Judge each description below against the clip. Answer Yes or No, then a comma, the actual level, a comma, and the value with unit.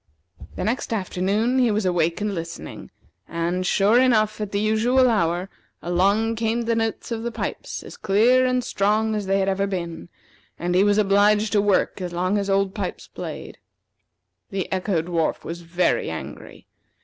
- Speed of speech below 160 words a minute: No, average, 175 wpm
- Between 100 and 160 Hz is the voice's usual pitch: No, high, 200 Hz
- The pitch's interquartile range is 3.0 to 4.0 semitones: Yes, average, 3.4 semitones